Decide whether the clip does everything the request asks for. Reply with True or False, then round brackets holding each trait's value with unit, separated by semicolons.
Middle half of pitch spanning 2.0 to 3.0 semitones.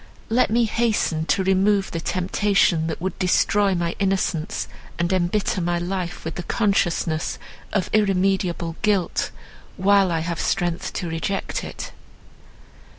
True (2.7 semitones)